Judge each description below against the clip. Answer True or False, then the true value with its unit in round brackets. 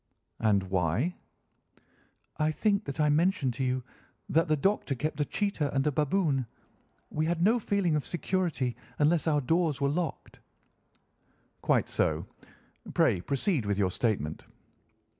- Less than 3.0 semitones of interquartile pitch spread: False (5.2 semitones)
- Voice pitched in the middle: True (150 Hz)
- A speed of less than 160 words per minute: True (140 wpm)